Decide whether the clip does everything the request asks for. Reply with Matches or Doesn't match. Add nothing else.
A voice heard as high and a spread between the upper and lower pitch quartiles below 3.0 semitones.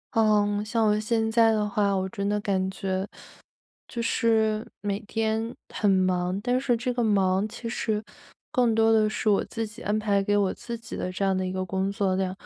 Matches